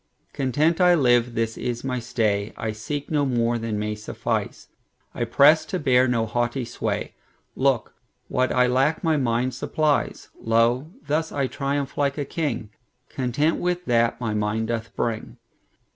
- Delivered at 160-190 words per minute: No, average, 140 wpm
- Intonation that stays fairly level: No, average, 3.8 semitones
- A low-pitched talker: Yes, low, 125 Hz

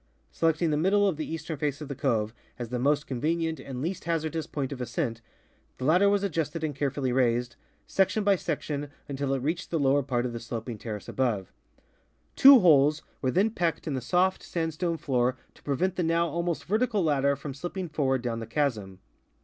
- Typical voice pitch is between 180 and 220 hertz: No, medium, 150 Hz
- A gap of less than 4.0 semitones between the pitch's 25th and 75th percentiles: No, average, 4.7 semitones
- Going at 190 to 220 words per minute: Yes, average, 200 wpm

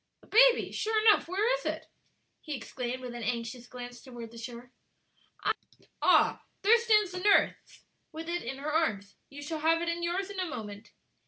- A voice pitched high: Yes, very high, 305 Hz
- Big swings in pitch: Yes, wide, 7.4 semitones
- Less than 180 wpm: No, average, 185 wpm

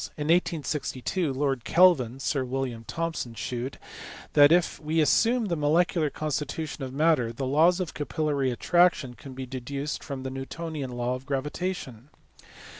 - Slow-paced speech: No, average, 145 wpm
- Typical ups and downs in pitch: Yes, average, 3.9 semitones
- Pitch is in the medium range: Yes, medium, 145 Hz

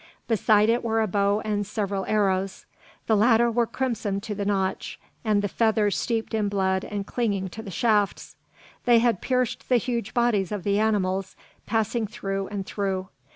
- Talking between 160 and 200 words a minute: Yes, average, 170 wpm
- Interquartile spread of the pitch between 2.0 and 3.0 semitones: Yes, narrow, 2.4 semitones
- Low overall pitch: No, high, 210 Hz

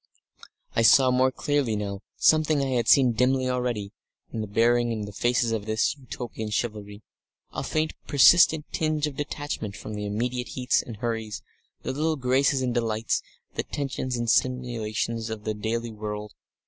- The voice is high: No, low, 120 Hz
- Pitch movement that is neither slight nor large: Yes, average, 3.3 semitones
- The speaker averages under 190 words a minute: Yes, average, 165 wpm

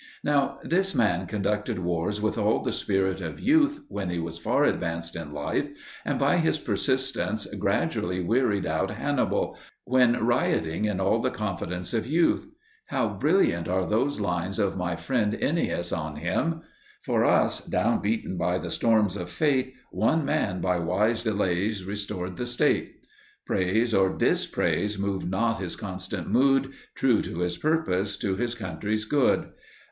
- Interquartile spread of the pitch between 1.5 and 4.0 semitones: No, average, 5.2 semitones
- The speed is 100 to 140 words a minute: No, average, 155 wpm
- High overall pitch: No, low, 100 Hz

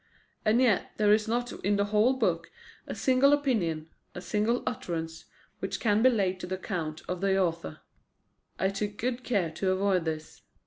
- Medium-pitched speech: No, high, 200 Hz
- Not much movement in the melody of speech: No, average, 4.7 semitones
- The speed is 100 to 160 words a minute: No, average, 180 wpm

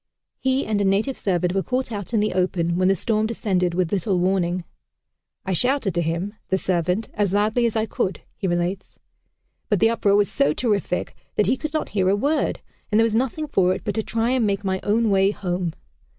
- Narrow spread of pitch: No, average, 3.5 semitones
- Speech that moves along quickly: Yes, fast, 220 wpm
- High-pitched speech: Yes, high, 200 Hz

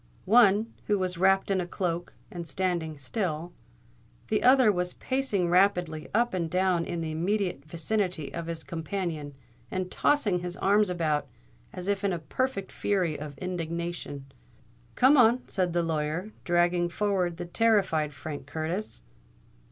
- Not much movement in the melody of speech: No, average, 3.3 semitones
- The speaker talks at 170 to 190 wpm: No, average, 150 wpm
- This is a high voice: No, medium, 180 Hz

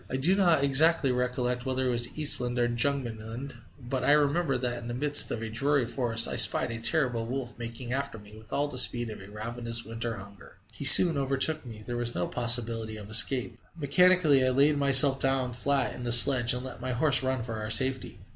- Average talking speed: No, fast, 210 wpm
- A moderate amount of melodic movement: Yes, average, 3.0 semitones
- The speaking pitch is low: Yes, low, 125 Hz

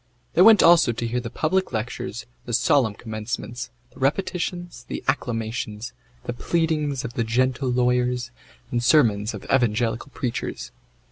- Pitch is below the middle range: Yes, low, 125 Hz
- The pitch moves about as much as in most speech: Yes, average, 3.5 semitones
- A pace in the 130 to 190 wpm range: Yes, average, 140 wpm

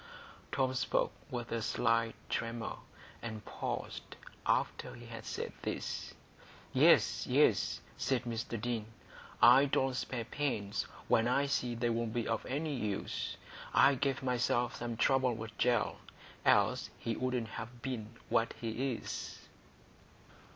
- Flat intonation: Yes, narrow, 2.1 semitones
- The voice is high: No, low, 120 Hz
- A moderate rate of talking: No, slow, 130 wpm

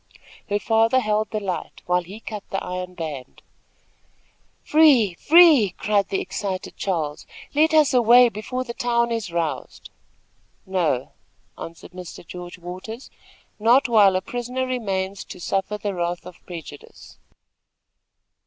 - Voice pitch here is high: Yes, high, 200 Hz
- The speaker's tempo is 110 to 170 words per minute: Yes, slow, 135 wpm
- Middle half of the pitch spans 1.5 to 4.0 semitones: No, average, 4.8 semitones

